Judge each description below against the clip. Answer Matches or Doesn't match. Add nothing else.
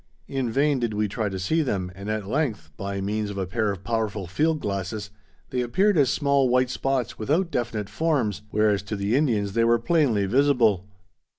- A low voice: Matches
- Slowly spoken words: Doesn't match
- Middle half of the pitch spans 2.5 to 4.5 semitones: Doesn't match